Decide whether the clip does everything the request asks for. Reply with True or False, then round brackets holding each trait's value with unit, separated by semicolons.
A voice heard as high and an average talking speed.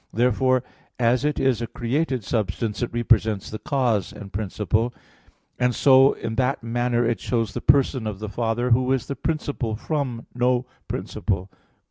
False (120 Hz; 160 wpm)